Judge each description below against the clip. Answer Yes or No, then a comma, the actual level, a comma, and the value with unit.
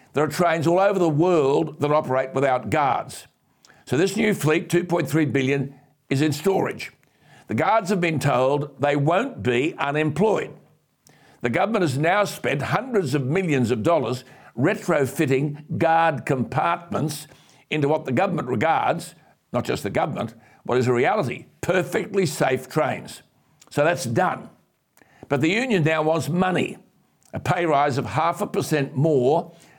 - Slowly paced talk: No, average, 150 wpm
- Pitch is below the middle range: No, medium, 155 Hz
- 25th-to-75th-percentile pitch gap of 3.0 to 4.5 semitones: Yes, average, 3.7 semitones